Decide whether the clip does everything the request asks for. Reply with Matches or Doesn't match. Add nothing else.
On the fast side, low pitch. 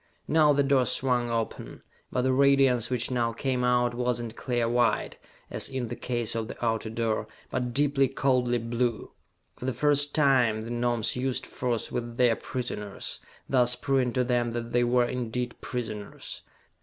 Doesn't match